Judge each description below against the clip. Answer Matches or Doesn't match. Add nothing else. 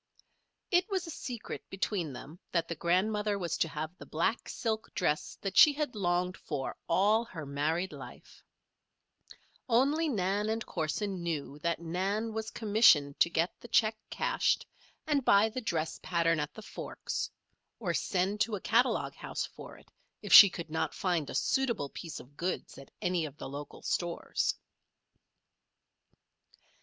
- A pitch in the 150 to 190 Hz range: Matches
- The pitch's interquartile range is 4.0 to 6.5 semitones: Matches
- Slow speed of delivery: Doesn't match